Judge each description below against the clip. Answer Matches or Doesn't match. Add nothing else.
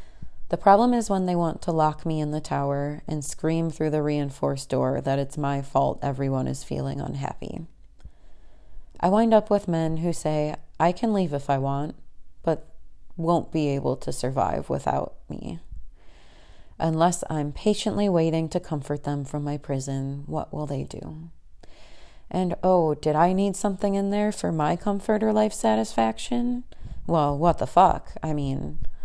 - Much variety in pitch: Doesn't match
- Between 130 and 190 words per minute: Matches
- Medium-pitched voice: Matches